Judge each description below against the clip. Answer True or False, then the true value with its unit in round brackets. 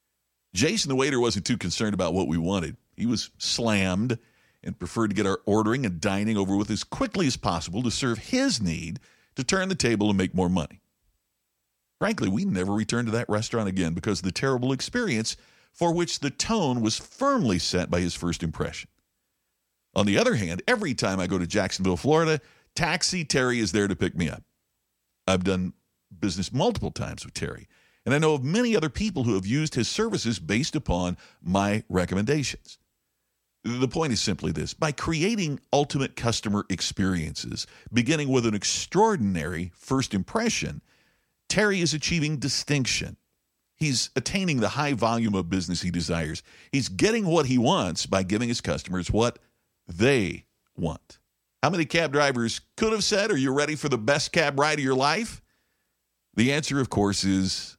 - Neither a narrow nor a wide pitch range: False (7.3 semitones)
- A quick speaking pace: False (175 wpm)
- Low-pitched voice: True (115 Hz)